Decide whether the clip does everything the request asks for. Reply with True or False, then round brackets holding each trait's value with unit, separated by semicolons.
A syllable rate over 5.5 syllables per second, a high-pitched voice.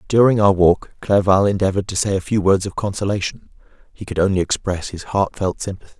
False (6.0 syllables/s; 95 Hz)